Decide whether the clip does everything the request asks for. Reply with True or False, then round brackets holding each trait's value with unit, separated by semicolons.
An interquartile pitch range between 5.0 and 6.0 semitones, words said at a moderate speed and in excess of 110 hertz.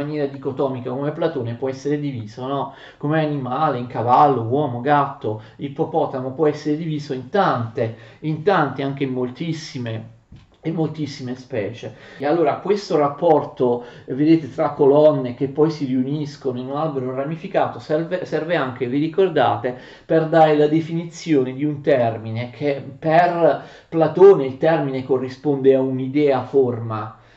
False (3.2 semitones; 140 wpm; 140 Hz)